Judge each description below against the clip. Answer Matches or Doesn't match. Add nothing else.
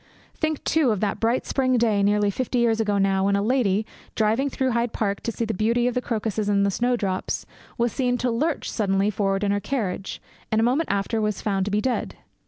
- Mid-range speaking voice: Doesn't match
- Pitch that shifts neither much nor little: Matches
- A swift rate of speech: Matches